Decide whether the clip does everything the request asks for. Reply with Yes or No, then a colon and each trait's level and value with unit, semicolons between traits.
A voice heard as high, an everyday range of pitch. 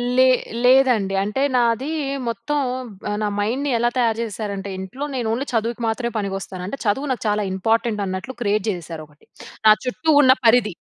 Yes: high, 225 Hz; average, 3.9 semitones